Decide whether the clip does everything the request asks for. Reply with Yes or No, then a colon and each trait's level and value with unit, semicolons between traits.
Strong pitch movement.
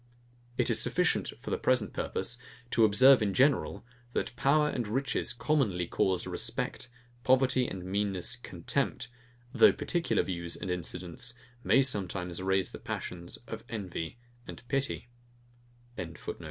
Yes: wide, 5.8 semitones